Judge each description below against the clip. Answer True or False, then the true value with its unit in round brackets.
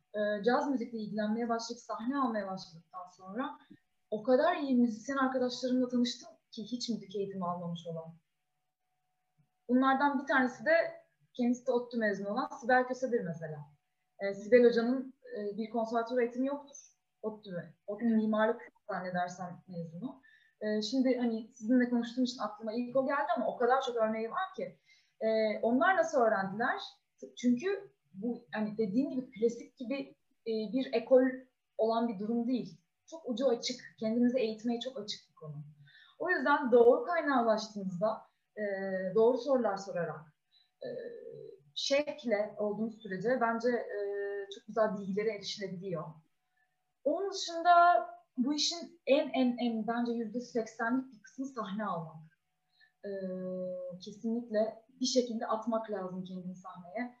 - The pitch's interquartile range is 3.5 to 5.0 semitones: True (4.5 semitones)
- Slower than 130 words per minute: False (135 wpm)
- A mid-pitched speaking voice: False (230 Hz)